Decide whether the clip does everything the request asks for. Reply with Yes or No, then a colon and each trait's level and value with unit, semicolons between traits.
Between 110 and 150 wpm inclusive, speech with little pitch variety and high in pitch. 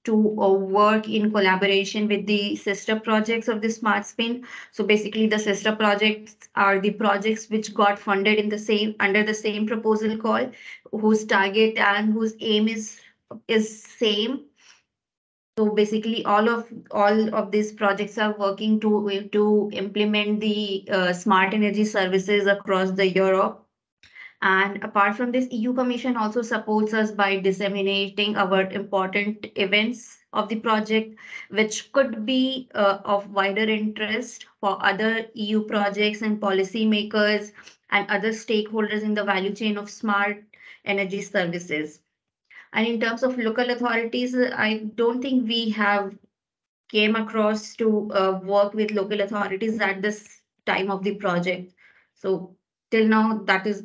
Yes: average, 145 wpm; narrow, 1.6 semitones; high, 210 Hz